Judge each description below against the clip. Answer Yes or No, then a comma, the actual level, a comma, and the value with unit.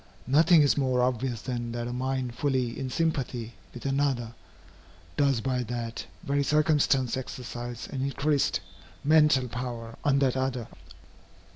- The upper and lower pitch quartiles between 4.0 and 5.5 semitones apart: No, narrow, 2.5 semitones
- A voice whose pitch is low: Yes, low, 130 Hz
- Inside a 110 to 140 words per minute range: Yes, slow, 135 wpm